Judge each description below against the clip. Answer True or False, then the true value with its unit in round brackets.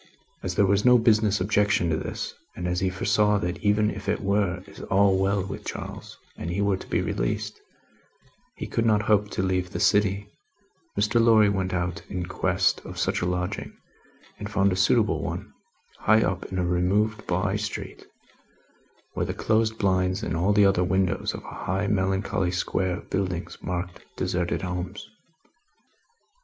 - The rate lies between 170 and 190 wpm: True (175 wpm)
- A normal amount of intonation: False (2.3 semitones)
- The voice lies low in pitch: True (95 Hz)